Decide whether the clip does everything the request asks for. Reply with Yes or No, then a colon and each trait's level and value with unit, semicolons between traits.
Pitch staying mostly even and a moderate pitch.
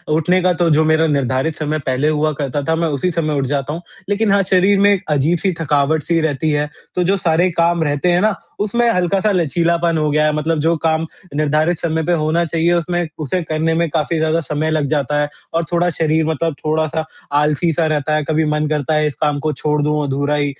Yes: narrow, 2.3 semitones; medium, 160 Hz